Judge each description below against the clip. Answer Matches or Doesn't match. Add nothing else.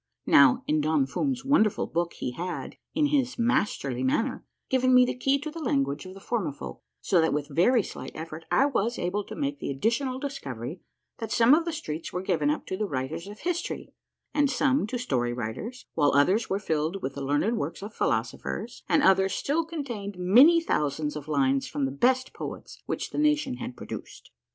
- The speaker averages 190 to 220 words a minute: Matches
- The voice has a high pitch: Matches